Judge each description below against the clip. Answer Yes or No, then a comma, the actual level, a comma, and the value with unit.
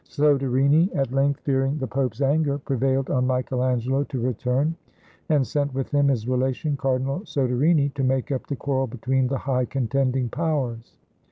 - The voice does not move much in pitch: Yes, narrow, 1.8 semitones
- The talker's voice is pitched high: No, low, 135 Hz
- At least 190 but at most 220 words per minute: No, average, 170 wpm